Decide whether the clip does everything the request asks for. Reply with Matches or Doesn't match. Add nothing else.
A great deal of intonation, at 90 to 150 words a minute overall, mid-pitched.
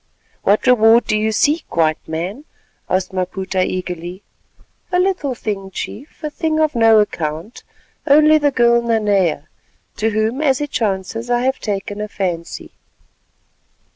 Doesn't match